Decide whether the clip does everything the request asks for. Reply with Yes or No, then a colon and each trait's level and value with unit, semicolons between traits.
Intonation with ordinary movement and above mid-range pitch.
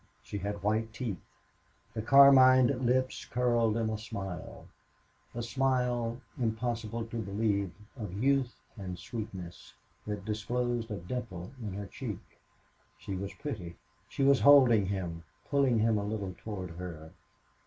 No: average, 3.7 semitones; low, 110 Hz